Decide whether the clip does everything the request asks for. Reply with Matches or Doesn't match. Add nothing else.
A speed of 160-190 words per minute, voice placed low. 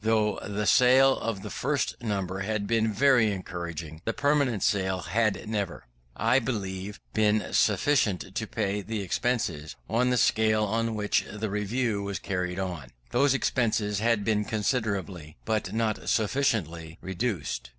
Doesn't match